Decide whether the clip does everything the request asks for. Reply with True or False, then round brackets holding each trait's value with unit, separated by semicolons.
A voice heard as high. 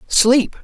True (255 Hz)